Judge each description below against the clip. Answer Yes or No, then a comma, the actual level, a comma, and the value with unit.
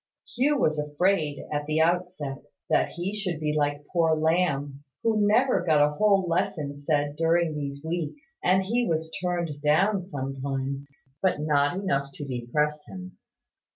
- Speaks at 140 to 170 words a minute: Yes, average, 155 wpm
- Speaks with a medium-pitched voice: Yes, medium, 155 Hz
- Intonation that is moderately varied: Yes, average, 3.9 semitones